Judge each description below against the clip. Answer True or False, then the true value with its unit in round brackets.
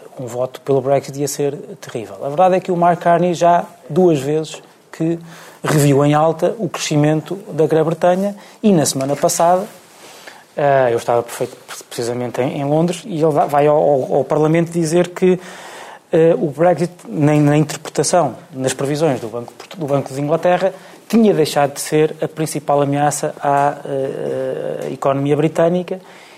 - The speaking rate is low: False (140 wpm)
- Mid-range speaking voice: True (155 Hz)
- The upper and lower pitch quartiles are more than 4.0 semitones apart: False (3.6 semitones)